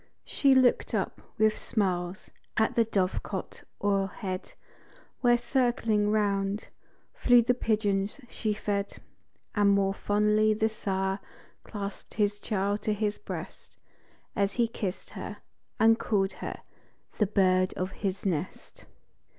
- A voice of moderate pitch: No, high, 205 Hz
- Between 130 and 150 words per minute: Yes, slow, 135 wpm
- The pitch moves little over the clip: Yes, narrow, 2.1 semitones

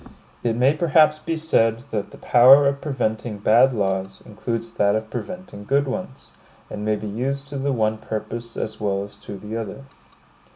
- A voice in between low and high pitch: No, low, 115 Hz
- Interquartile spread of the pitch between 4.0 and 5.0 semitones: Yes, average, 4.6 semitones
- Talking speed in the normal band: Yes, average, 180 wpm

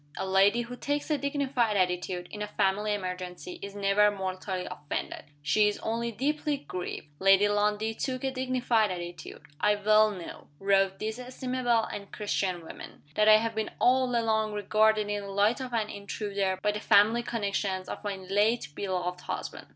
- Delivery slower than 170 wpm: No, average, 175 wpm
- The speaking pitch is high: Yes, high, 210 Hz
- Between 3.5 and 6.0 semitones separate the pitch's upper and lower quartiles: No, average, 3.0 semitones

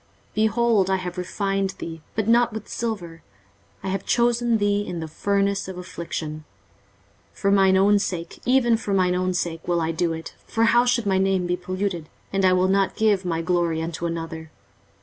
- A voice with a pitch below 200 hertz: Yes, high, 190 Hz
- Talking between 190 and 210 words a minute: Yes, average, 195 wpm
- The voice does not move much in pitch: No, average, 3.1 semitones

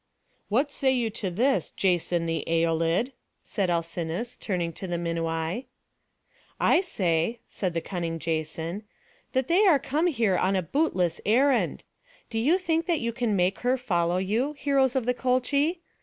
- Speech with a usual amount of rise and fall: No, wide, 7.7 semitones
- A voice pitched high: Yes, high, 210 Hz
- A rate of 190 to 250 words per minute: No, average, 160 wpm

